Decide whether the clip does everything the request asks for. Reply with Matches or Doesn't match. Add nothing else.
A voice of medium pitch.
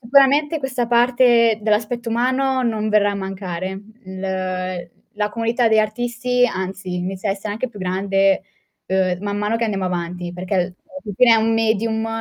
Doesn't match